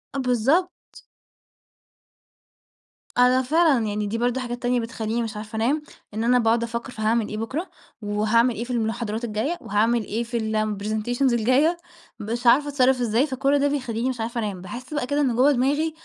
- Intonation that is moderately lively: Yes, average, 3.0 semitones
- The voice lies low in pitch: No, high, 240 Hz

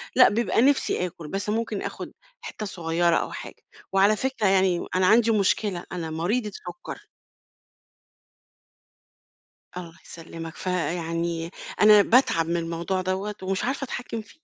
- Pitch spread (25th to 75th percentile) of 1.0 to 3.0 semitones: No, average, 4.1 semitones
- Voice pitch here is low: No, high, 190 Hz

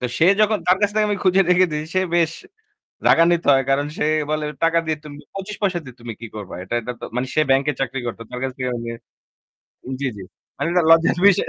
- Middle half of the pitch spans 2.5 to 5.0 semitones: No, wide, 5.5 semitones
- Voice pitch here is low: No, medium, 155 Hz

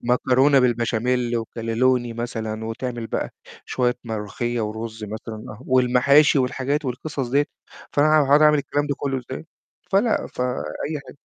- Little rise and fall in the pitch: No, average, 3.4 semitones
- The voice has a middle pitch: No, low, 125 Hz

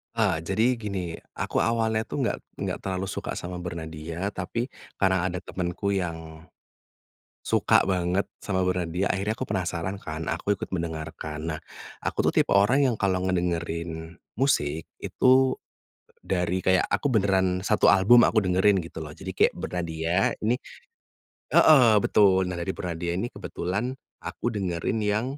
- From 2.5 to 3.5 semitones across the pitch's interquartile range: Yes, average, 3.2 semitones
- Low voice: Yes, very low, 95 Hz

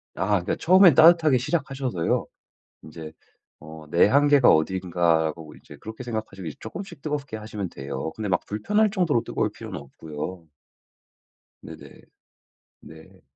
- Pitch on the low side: Yes, low, 105 Hz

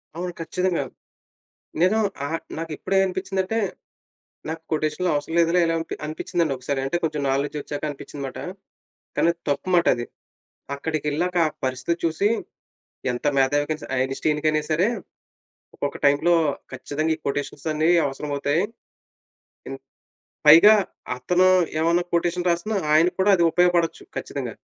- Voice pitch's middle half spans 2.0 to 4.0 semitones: Yes, average, 3.4 semitones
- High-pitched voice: No, medium, 160 Hz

